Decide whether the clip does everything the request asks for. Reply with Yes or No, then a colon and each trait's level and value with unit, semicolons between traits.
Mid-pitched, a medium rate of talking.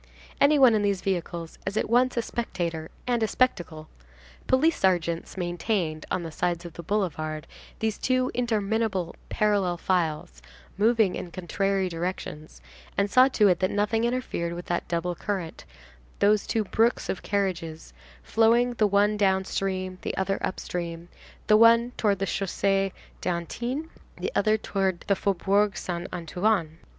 No: high, 195 Hz; average, 150 wpm